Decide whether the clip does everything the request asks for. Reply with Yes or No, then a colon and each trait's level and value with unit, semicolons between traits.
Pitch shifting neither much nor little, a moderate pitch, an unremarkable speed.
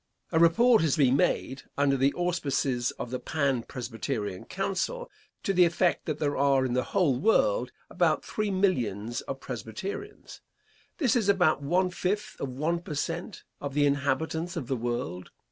No: wide, 5.7 semitones; medium, 145 Hz; average, 165 wpm